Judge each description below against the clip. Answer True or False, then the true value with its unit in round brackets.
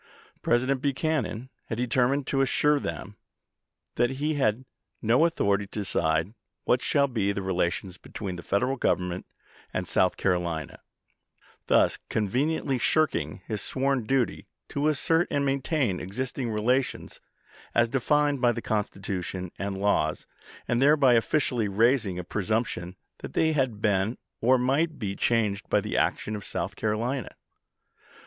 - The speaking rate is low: False (145 wpm)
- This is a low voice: True (115 Hz)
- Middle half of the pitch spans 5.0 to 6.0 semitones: True (5.4 semitones)